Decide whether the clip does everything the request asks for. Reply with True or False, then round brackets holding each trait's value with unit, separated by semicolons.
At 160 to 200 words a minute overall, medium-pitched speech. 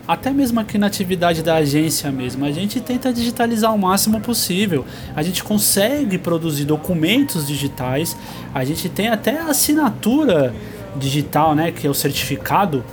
False (150 wpm; 170 Hz)